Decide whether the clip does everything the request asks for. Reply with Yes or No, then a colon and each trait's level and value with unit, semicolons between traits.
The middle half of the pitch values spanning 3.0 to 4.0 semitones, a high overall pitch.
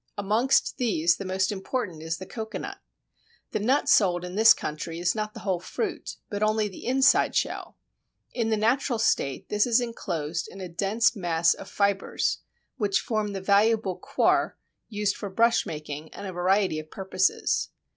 Yes: average, 3.7 semitones; high, 200 Hz